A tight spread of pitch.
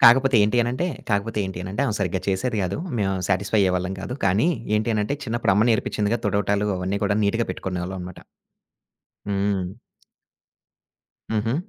No: average, 3.0 semitones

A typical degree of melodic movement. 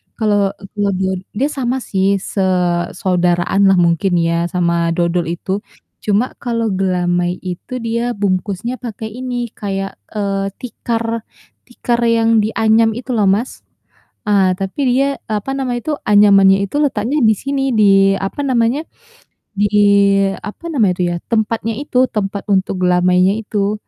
Yes: average, 3.7 semitones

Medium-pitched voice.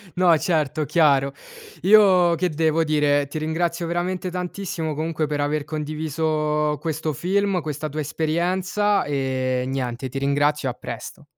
Yes: medium, 155 Hz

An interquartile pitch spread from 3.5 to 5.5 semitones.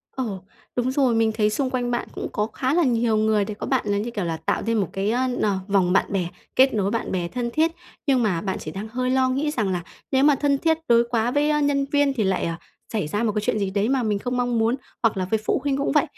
Yes: average, 4.3 semitones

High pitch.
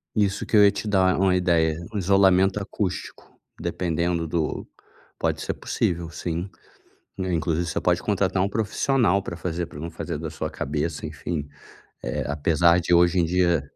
No: very low, 85 Hz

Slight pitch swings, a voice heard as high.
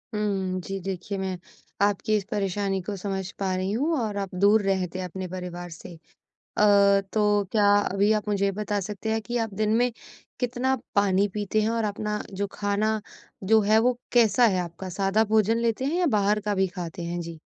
Yes: narrow, 2.3 semitones; high, 205 Hz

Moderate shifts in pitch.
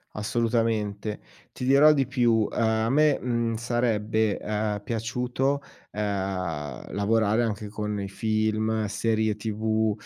No: narrow, 1.9 semitones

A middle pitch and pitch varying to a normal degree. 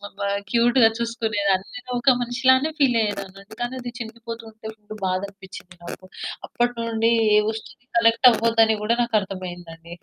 No: high, 225 Hz; average, 3.1 semitones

